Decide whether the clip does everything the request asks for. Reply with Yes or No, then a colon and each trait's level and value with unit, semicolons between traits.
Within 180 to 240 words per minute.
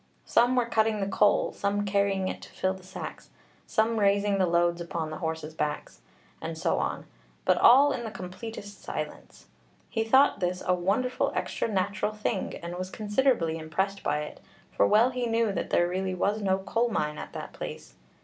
Yes: average, 190 wpm